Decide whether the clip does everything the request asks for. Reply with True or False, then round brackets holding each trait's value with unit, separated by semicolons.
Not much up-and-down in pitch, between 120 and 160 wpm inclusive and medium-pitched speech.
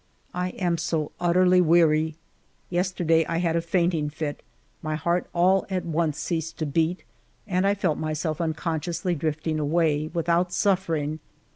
True (2.3 semitones; 150 wpm; 165 Hz)